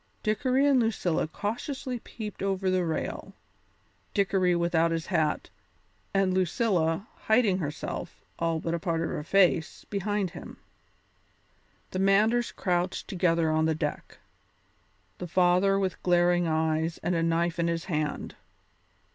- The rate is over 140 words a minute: No, slow, 135 wpm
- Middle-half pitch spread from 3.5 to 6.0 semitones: No, average, 3.1 semitones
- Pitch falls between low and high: Yes, medium, 180 Hz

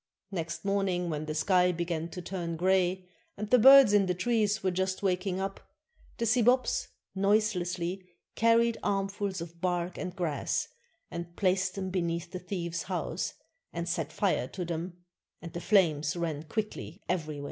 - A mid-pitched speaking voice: Yes, medium, 180 Hz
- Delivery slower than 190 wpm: Yes, average, 160 wpm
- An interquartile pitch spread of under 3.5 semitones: Yes, narrow, 2.6 semitones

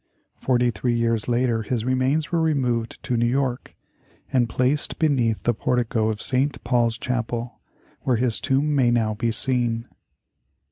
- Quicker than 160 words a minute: No, average, 150 wpm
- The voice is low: Yes, low, 120 Hz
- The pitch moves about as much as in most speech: No, narrow, 1.9 semitones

